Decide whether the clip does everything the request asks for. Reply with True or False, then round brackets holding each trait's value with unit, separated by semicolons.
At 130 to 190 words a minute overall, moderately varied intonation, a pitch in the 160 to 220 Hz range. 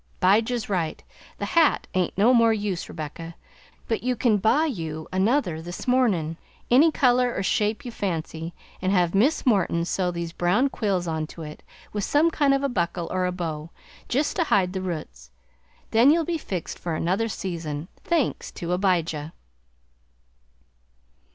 False (165 wpm; 6.3 semitones; 190 Hz)